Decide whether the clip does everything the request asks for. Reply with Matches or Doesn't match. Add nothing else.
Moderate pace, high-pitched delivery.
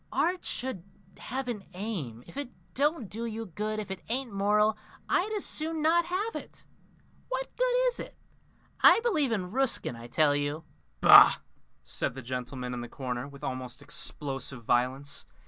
Matches